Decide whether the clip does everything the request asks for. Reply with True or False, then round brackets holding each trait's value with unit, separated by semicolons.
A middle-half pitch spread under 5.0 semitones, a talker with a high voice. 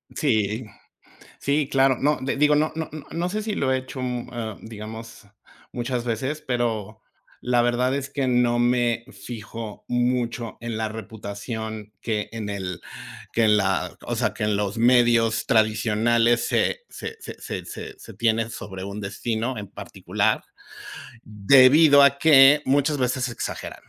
False (3.3 semitones; 120 Hz)